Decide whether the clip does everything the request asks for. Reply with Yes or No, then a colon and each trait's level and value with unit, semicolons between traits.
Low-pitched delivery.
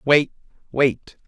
Yes: low, 130 Hz